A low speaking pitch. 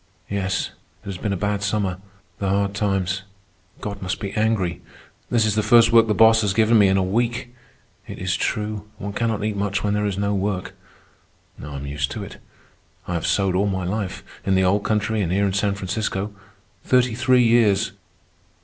Yes: low, 100 Hz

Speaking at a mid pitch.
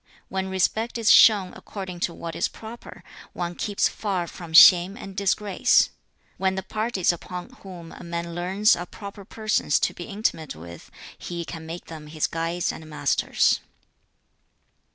Yes: medium, 180 Hz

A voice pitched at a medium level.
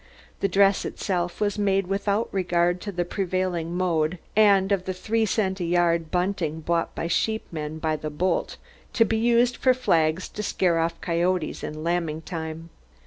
Yes: medium, 180 Hz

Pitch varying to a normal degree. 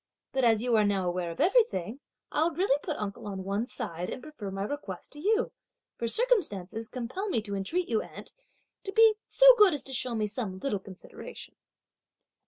No: wide, 8.8 semitones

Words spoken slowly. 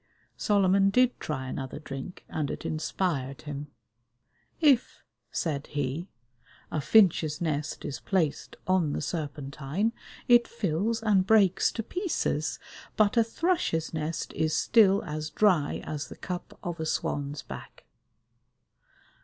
Yes: slow, 130 wpm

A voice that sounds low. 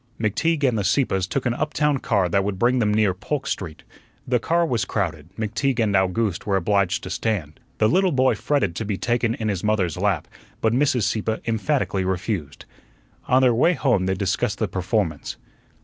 Yes: low, 110 Hz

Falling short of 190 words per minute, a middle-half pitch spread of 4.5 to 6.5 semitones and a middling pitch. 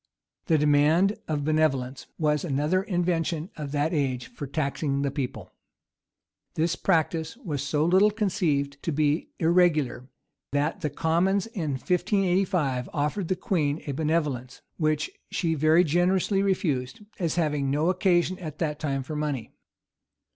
No: average, 140 wpm; average, 3.6 semitones; medium, 155 Hz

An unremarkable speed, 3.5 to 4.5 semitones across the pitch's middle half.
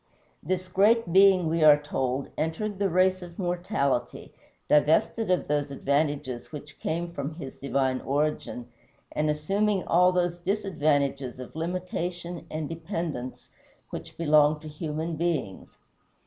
No: slow, 130 wpm; average, 3.8 semitones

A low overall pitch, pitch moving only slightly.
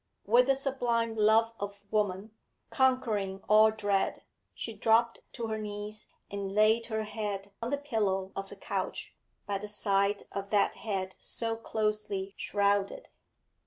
No: high, 210 Hz; narrow, 2.2 semitones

